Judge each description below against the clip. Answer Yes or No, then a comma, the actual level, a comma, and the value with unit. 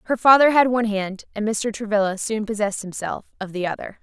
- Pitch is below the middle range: No, high, 215 Hz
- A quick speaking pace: Yes, fast, 210 wpm